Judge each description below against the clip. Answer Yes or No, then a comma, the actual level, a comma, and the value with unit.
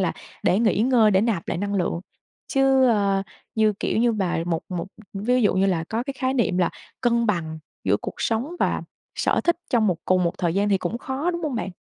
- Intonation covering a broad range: No, average, 4.8 semitones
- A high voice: Yes, high, 210 Hz